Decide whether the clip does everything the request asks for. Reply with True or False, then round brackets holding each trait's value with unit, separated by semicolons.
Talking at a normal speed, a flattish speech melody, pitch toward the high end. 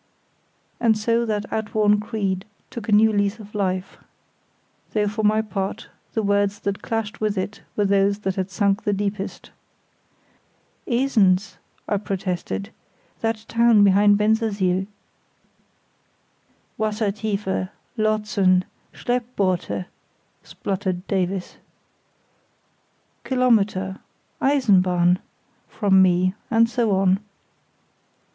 False (95 wpm; 2.3 semitones; 205 Hz)